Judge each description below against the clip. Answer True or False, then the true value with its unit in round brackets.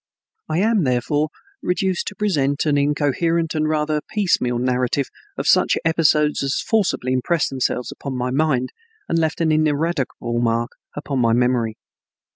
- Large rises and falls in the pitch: False (4.4 semitones)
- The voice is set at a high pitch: False (145 Hz)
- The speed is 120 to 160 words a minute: True (145 wpm)